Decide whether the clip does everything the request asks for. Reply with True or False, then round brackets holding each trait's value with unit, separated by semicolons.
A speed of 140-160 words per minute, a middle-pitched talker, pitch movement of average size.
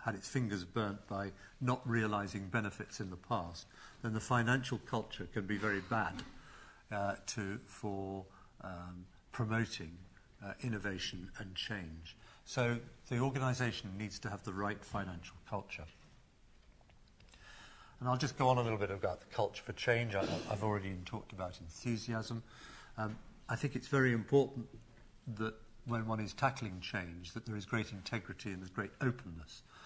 False (155 wpm; 110 Hz; 3.3 semitones)